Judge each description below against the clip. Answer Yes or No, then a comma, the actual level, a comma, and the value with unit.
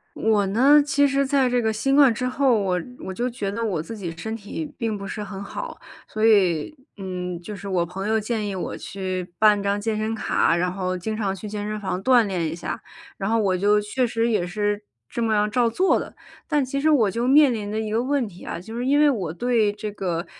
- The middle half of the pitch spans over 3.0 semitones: Yes, average, 3.8 semitones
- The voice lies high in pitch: Yes, high, 215 Hz